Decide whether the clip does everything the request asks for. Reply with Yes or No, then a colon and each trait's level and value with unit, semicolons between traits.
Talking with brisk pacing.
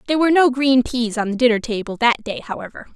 Yes: fast, 245 wpm